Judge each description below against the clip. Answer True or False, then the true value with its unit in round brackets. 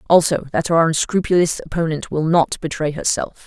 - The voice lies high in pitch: False (160 Hz)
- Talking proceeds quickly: False (155 wpm)